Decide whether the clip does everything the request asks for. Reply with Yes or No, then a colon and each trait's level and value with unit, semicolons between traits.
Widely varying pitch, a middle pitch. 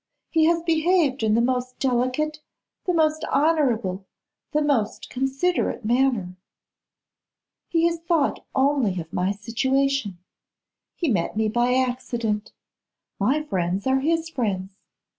No: wide, 6.1 semitones; very high, 260 Hz